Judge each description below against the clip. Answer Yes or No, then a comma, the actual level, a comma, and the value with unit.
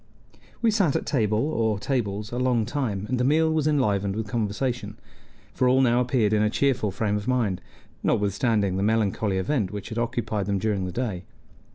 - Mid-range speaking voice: No, low, 110 Hz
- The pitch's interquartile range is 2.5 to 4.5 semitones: Yes, average, 3.8 semitones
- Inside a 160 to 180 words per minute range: No, average, 190 wpm